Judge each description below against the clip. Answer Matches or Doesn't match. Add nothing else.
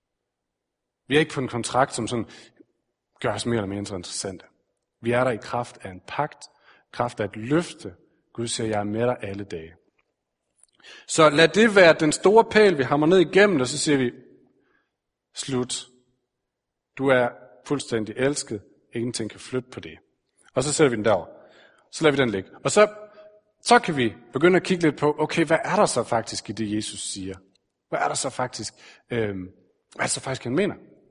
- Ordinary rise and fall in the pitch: Doesn't match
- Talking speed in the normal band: Matches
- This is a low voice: Matches